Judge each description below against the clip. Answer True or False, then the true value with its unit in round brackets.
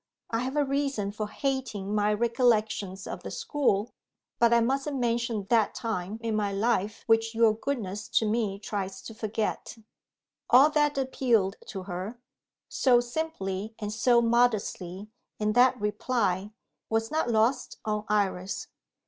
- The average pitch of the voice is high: True (225 Hz)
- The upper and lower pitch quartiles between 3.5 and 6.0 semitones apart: False (3.0 semitones)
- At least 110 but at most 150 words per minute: True (145 wpm)